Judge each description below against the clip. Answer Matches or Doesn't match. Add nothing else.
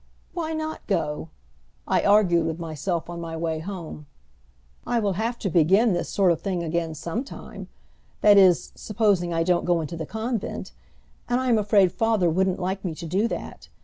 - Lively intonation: Doesn't match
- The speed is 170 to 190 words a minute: Matches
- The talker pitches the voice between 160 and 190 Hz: Matches